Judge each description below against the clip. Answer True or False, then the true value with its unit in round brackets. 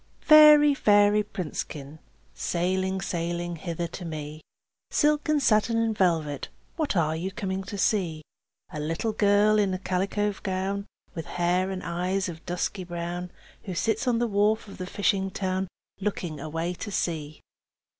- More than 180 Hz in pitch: True (190 Hz)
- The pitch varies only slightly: False (3.3 semitones)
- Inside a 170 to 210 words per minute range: False (155 wpm)